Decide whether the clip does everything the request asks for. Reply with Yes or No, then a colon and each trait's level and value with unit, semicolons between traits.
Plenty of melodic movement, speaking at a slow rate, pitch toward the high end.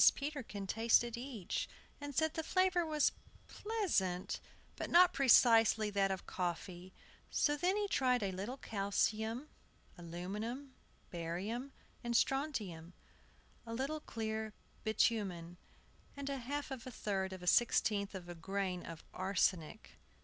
Yes: wide, 6.3 semitones; slow, 130 wpm; high, 220 Hz